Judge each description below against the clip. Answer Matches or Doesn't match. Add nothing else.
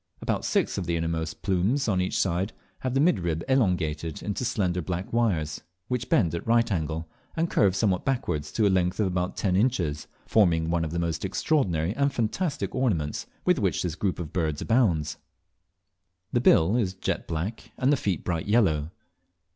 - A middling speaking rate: Matches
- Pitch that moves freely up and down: Matches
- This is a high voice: Doesn't match